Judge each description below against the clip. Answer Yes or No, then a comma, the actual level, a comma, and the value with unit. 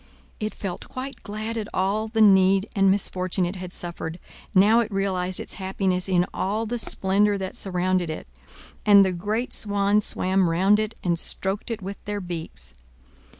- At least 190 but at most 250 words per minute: No, average, 170 wpm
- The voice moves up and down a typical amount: No, narrow, 2.3 semitones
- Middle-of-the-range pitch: No, high, 195 Hz